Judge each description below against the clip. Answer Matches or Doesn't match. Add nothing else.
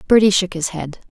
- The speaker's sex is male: Doesn't match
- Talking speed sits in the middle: Doesn't match